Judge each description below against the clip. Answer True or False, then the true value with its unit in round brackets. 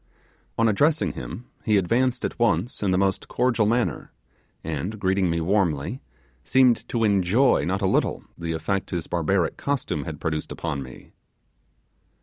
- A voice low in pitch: True (100 Hz)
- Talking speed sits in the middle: True (150 wpm)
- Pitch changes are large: True (5.7 semitones)